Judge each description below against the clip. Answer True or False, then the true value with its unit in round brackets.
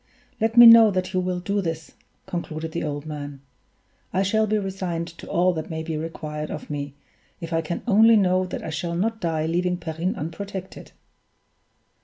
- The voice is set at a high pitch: False (175 Hz)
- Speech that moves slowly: False (185 wpm)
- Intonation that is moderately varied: True (3.3 semitones)